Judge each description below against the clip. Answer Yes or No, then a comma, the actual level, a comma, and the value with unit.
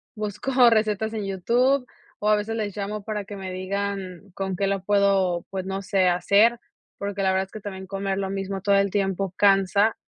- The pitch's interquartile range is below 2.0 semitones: Yes, narrow, 1.6 semitones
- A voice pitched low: No, high, 200 Hz